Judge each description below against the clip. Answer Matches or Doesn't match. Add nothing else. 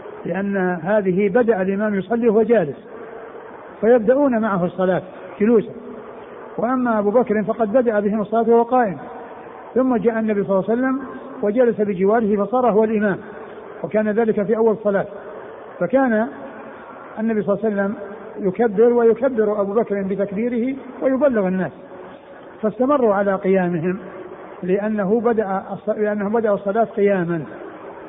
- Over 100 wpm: Matches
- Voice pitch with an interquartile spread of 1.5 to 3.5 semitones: Matches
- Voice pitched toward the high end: Matches